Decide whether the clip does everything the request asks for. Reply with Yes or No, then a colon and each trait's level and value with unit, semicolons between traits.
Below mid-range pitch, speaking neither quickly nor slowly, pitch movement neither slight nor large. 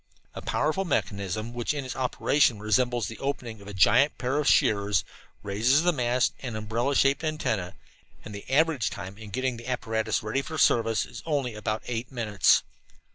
Yes: low, 120 Hz; average, 180 wpm; average, 4.2 semitones